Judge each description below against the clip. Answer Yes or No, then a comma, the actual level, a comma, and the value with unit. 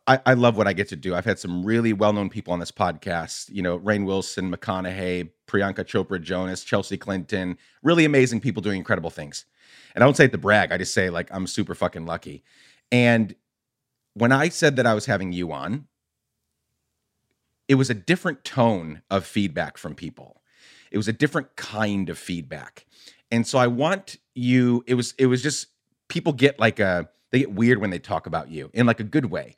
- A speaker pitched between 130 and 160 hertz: No, low, 105 Hz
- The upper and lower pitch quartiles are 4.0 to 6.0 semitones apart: Yes, average, 5.1 semitones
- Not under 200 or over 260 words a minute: Yes, fast, 205 wpm